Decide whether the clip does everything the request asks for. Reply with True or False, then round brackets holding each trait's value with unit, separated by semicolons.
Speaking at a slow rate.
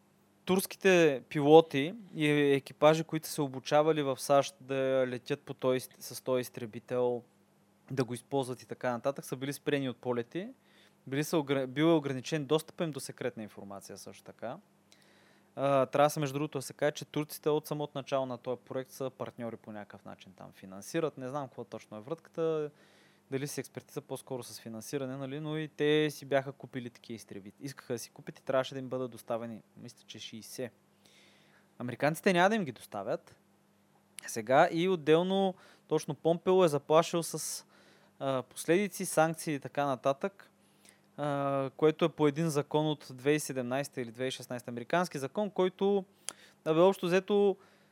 False (160 wpm)